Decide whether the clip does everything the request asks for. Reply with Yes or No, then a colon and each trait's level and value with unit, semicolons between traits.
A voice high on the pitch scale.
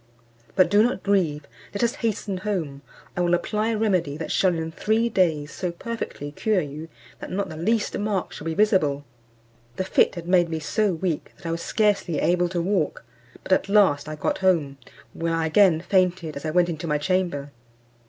No: medium, 175 Hz